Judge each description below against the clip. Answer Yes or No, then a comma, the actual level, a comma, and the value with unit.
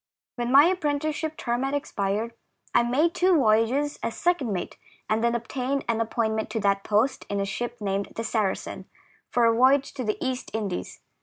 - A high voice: Yes, high, 235 Hz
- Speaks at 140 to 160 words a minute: No, average, 185 wpm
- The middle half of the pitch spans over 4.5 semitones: No, average, 4.2 semitones